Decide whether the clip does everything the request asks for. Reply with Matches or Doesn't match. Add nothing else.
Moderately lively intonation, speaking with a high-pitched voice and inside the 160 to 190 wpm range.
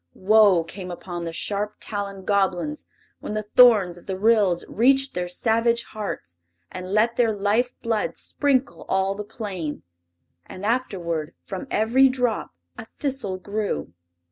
Doesn't match